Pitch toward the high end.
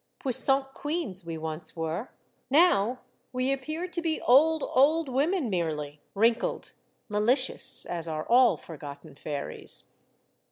Yes: high, 245 Hz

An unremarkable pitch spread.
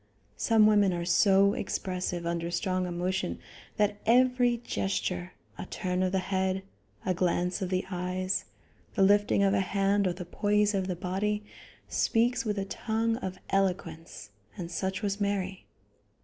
No: narrow, 2.2 semitones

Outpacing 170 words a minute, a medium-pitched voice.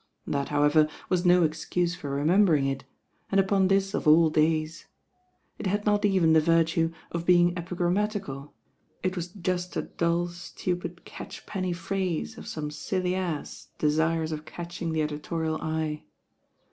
No: average, 150 wpm; medium, 170 Hz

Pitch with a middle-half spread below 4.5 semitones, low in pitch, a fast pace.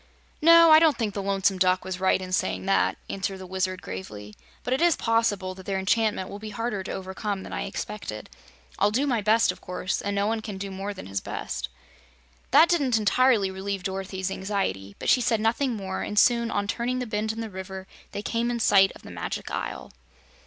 No: average, 3.2 semitones; high, 200 Hz; fast, 215 wpm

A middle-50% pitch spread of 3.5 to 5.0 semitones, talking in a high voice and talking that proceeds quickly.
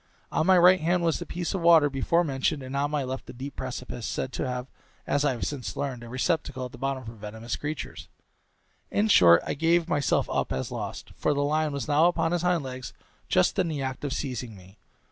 No: average, 4.3 semitones; medium, 140 Hz; fast, 230 wpm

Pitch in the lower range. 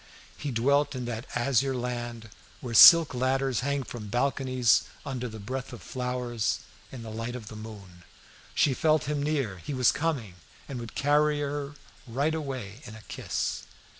Yes: low, 125 Hz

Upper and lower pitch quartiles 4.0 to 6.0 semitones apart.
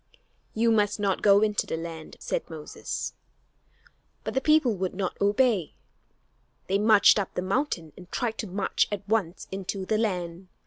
No: average, 3.2 semitones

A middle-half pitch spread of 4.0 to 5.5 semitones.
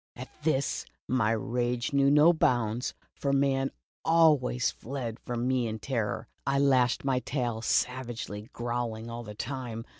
No: average, 2.8 semitones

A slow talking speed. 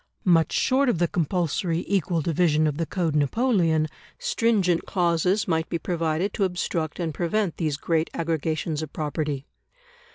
No: average, 150 wpm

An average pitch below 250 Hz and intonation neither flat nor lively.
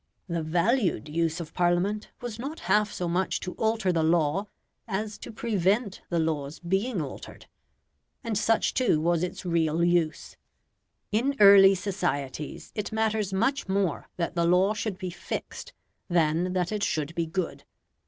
Yes: medium, 185 Hz; average, 3.9 semitones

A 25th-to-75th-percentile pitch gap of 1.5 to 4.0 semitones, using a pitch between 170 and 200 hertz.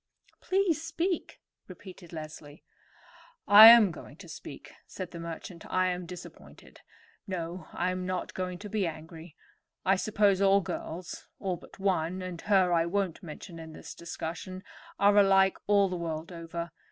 Yes: average, 2.8 semitones; medium, 185 Hz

